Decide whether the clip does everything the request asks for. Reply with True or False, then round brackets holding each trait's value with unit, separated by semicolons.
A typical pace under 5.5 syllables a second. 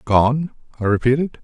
True (4.7 syllables/s)